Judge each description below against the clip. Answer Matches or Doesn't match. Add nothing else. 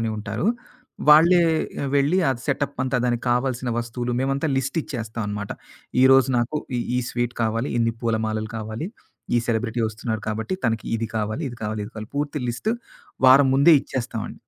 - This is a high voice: Doesn't match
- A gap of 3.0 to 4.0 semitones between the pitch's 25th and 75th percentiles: Matches